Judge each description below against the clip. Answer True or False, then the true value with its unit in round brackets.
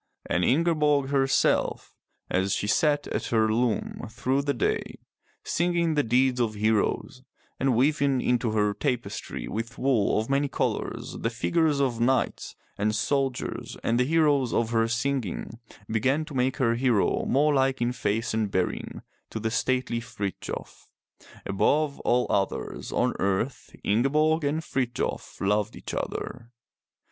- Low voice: True (125 Hz)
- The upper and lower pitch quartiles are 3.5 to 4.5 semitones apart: True (3.8 semitones)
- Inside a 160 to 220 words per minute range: False (145 wpm)